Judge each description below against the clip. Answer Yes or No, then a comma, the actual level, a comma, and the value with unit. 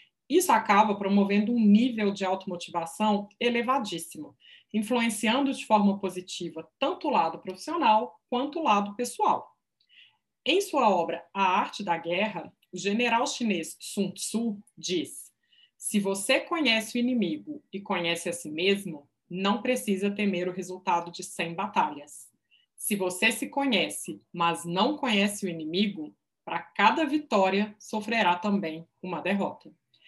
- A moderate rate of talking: Yes, average, 135 wpm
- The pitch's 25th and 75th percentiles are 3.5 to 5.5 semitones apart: Yes, average, 5.0 semitones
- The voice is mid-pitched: No, high, 200 Hz